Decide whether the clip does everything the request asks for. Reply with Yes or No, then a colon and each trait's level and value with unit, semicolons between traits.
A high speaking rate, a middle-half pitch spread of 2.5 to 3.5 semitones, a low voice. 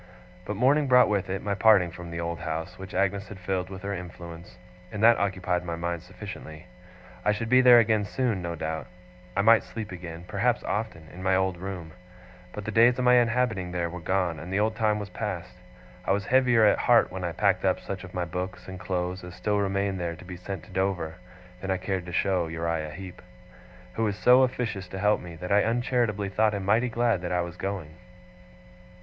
Yes: fast, 220 wpm; average, 3.1 semitones; very low, 95 Hz